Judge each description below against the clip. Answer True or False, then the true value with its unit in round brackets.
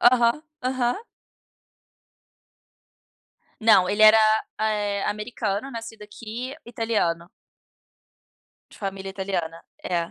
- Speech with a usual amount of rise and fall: True (3.2 semitones)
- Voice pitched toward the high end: True (215 Hz)